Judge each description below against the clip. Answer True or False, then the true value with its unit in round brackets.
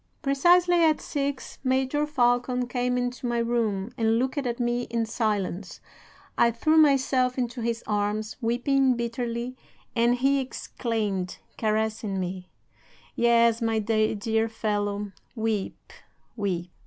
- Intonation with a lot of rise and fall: False (2.8 semitones)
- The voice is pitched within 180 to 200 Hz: False (235 Hz)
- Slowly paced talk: True (120 wpm)